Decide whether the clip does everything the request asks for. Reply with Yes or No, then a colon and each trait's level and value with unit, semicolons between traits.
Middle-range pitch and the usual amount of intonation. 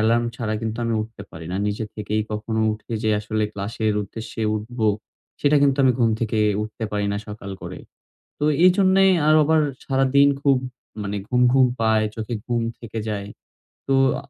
No: low, 115 Hz; average, 3.6 semitones